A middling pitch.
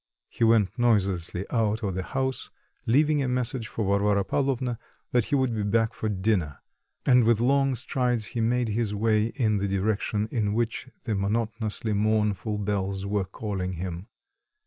No: low, 110 Hz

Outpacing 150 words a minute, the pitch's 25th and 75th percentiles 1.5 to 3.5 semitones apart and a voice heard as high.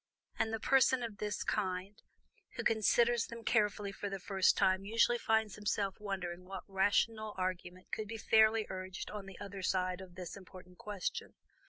Yes: average, 170 wpm; average, 2.7 semitones; high, 200 Hz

